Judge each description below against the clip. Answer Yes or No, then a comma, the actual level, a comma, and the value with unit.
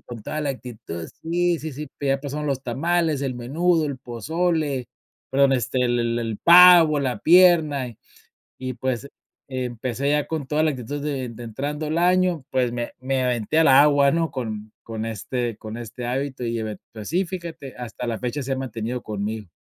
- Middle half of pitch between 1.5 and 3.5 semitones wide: No, average, 4.3 semitones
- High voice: No, low, 135 Hz